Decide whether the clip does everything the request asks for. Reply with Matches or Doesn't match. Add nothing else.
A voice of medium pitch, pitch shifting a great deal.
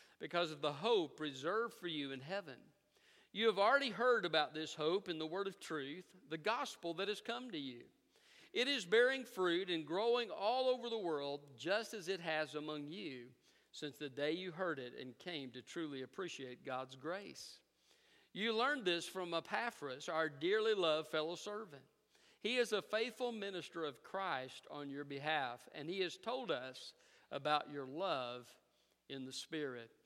Matches